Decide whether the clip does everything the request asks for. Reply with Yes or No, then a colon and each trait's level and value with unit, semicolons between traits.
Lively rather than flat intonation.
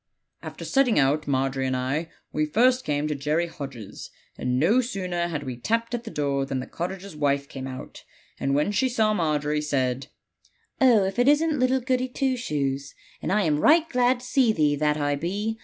Yes: wide, 9.0 semitones